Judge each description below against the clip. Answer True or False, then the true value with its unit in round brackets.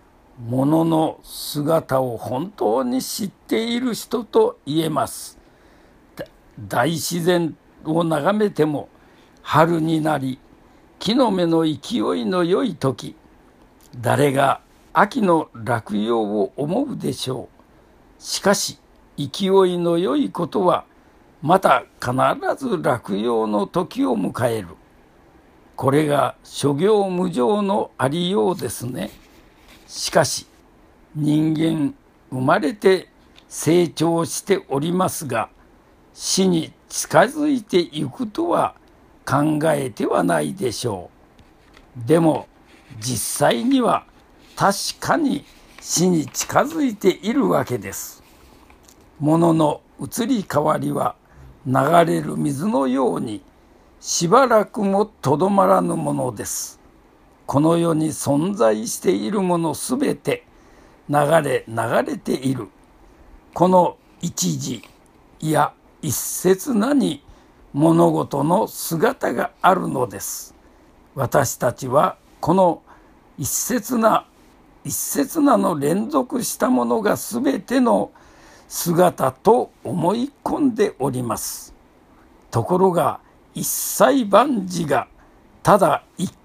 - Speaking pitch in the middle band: True (170 Hz)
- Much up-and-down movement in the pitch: True (6.5 semitones)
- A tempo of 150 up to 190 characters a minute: True (185 characters per minute)